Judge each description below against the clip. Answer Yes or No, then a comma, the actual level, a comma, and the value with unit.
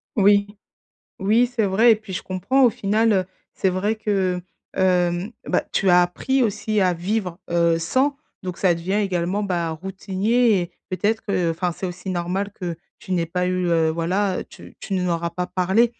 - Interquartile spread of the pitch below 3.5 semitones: Yes, average, 2.9 semitones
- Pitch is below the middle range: No, medium, 185 Hz